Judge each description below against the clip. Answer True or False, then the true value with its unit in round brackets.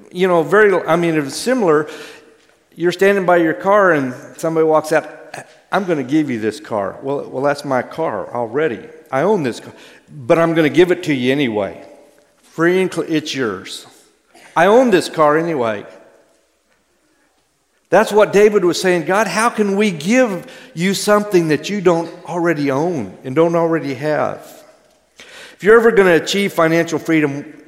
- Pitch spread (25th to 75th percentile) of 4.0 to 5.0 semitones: True (4.5 semitones)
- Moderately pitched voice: True (170 Hz)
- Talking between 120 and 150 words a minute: False (190 wpm)